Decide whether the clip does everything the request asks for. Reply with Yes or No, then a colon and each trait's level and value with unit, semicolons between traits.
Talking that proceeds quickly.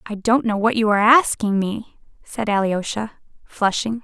No: average, 165 wpm